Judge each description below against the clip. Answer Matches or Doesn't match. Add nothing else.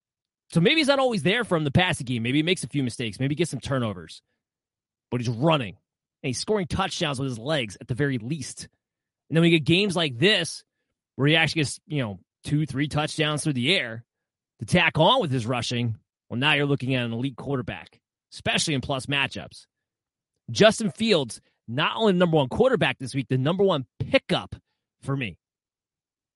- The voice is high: Doesn't match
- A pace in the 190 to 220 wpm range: Matches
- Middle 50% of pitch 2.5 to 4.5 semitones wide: Doesn't match